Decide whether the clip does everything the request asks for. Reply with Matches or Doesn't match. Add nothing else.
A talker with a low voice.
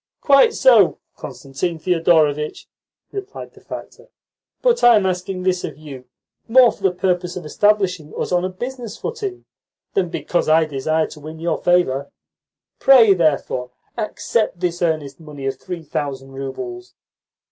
Doesn't match